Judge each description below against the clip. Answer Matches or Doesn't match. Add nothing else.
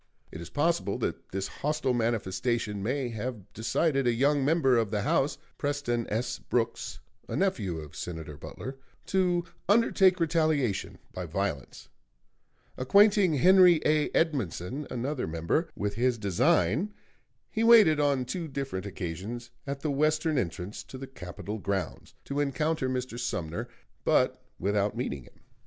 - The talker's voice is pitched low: Matches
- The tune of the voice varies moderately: Doesn't match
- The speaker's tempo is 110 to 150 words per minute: Matches